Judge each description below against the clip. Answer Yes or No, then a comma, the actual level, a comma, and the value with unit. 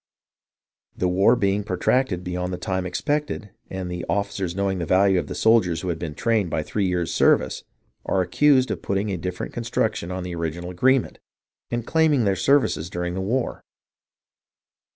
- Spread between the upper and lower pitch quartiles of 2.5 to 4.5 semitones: Yes, average, 4.2 semitones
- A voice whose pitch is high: No, very low, 95 Hz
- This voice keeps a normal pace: Yes, average, 170 wpm